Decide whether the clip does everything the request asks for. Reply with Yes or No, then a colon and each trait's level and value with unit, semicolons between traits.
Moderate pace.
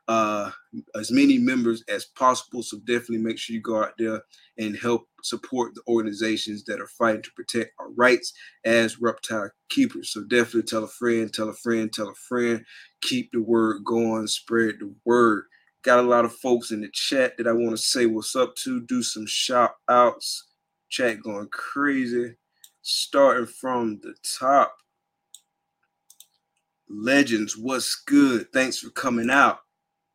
Yes: average, 160 wpm